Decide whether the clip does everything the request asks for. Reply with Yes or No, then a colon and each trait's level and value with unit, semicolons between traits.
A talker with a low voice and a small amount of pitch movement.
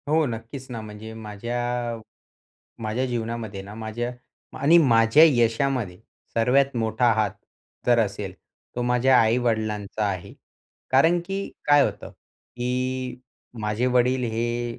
Yes: low, 120 Hz; narrow, 2.2 semitones